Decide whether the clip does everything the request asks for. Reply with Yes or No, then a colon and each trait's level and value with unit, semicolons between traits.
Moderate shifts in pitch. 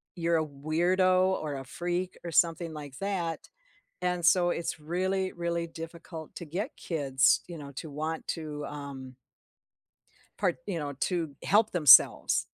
Yes: average, 3.0 semitones